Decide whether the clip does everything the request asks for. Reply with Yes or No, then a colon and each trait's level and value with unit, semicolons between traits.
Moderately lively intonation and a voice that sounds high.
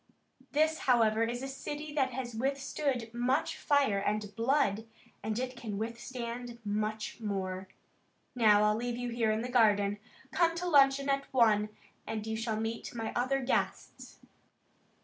Yes: average, 3.7 semitones; high, 235 Hz